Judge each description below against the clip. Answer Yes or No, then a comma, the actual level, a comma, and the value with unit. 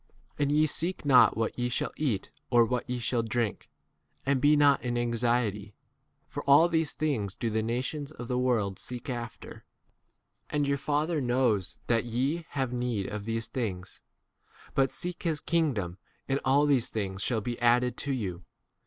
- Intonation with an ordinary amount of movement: Yes, average, 3.9 semitones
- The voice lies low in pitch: Yes, low, 125 Hz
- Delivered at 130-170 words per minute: No, average, 180 wpm